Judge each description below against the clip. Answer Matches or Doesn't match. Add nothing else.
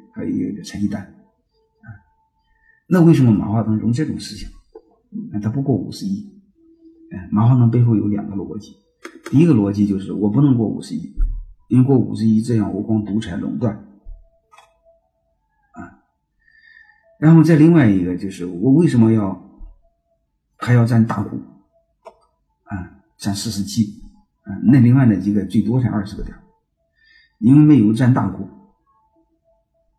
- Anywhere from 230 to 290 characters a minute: Doesn't match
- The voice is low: Matches